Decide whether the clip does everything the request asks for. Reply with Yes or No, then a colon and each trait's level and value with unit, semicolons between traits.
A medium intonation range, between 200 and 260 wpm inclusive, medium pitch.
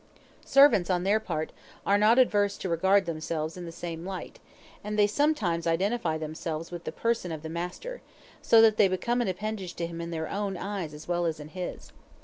Yes: average, 3.9 semitones; fast, 205 wpm; medium, 180 Hz